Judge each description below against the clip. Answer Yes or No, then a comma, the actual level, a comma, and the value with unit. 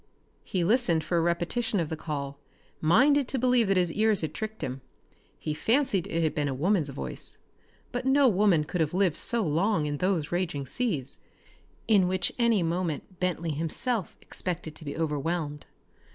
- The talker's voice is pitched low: No, medium, 175 Hz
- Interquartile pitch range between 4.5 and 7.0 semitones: Yes, wide, 5.6 semitones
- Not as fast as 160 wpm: No, average, 175 wpm